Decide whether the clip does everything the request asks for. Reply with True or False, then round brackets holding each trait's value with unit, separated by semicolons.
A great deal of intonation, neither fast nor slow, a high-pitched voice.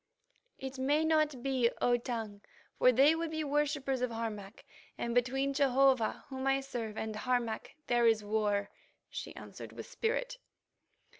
False (3.4 semitones; 150 wpm; 255 Hz)